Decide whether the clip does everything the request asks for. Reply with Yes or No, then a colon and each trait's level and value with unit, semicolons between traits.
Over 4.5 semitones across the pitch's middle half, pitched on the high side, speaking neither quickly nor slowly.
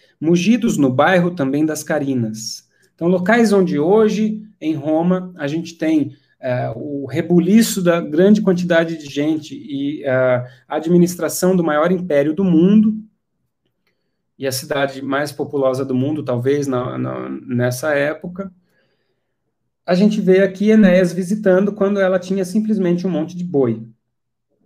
No: average, 5.2 semitones; medium, 165 Hz; average, 140 wpm